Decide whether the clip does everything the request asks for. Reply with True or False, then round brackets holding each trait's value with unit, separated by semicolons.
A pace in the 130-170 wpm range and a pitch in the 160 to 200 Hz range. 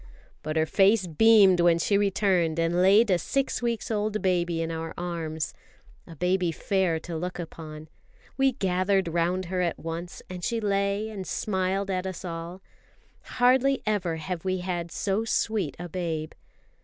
True (165 wpm; 185 Hz)